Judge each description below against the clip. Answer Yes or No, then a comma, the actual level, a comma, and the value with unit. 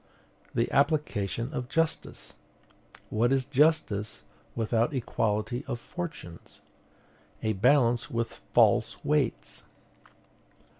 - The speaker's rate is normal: No, slow, 90 wpm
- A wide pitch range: No, average, 4.5 semitones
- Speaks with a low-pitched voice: Yes, low, 120 Hz